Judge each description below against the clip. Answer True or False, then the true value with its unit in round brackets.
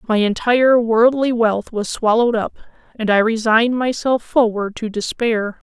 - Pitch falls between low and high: False (225 Hz)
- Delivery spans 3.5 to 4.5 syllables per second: False (4.8 syllables/s)